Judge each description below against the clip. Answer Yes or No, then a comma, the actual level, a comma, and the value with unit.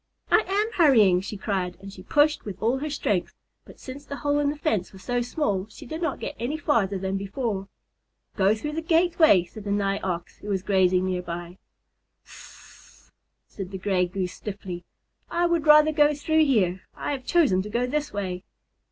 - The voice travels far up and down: Yes, wide, 7.6 semitones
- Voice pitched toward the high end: Yes, high, 210 Hz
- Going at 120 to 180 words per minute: No, average, 195 wpm